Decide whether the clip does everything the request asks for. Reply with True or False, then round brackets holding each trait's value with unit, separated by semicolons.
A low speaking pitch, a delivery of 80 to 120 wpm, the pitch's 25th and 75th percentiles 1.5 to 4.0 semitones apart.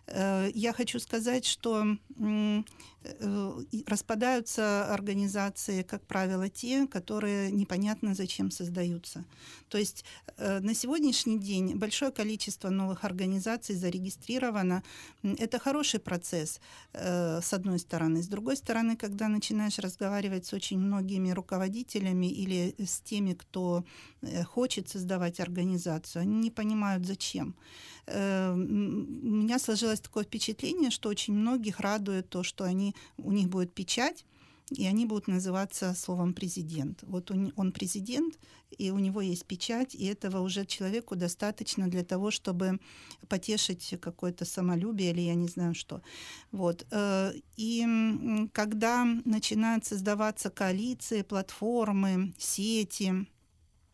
False (200 Hz; 115 wpm; 2.8 semitones)